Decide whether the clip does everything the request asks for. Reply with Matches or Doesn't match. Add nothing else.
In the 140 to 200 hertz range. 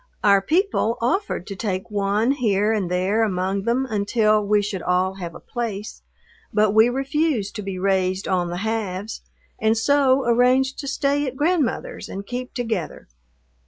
Doesn't match